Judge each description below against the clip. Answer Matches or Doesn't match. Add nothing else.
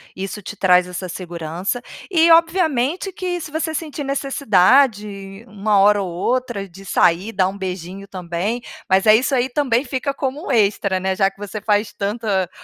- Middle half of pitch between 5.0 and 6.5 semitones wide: Matches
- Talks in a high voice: Matches